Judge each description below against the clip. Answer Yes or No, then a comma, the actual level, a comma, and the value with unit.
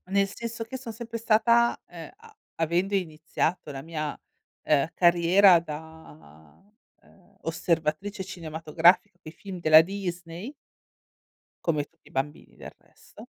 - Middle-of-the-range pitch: Yes, medium, 175 Hz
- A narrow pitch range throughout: No, average, 4.2 semitones